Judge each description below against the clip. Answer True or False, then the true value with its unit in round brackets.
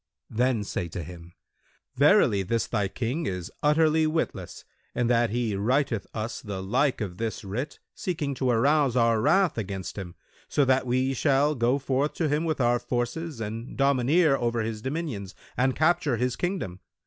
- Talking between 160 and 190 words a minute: True (170 wpm)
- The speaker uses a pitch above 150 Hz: False (125 Hz)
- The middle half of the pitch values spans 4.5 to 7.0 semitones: True (5.0 semitones)